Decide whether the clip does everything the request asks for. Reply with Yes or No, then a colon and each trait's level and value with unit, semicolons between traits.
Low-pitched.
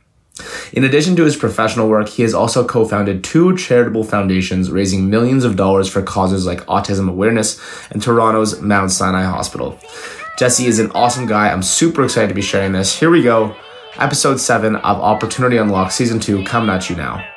Yes: low, 110 Hz